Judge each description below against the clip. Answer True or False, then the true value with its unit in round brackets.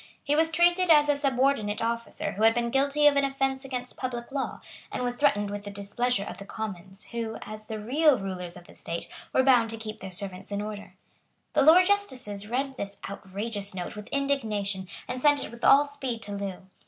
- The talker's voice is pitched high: True (235 Hz)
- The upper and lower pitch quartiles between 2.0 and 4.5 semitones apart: False (5.3 semitones)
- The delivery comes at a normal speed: False (210 wpm)